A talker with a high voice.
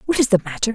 Yes: high, 215 Hz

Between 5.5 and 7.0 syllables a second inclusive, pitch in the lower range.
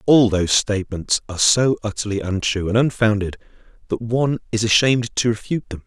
Yes: 6.1 syllables/s; low, 110 Hz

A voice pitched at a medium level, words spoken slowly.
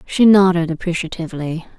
Yes: medium, 175 Hz; slow, 100 wpm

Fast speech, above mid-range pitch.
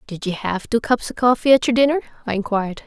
Yes: fast, 250 wpm; high, 230 Hz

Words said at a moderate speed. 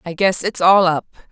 No: fast, 230 wpm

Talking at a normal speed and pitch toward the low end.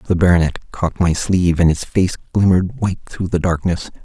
Yes: average, 195 wpm; very low, 90 Hz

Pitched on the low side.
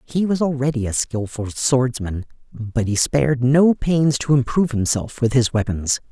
Yes: low, 125 Hz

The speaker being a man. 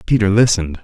Yes: male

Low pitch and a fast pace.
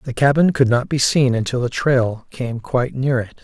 Yes: low, 125 Hz; fast, 225 wpm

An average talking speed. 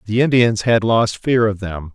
No: fast, 215 wpm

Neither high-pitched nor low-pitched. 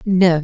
Yes: medium, 180 Hz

